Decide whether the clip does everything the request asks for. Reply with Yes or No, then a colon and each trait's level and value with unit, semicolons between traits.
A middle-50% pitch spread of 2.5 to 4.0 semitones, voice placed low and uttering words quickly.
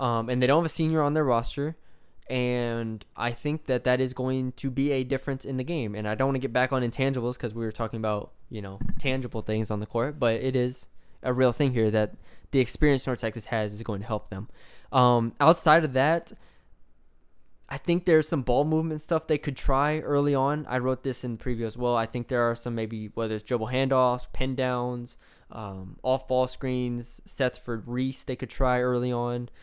Yes: average, 2.8 semitones; low, 125 Hz; fast, 225 wpm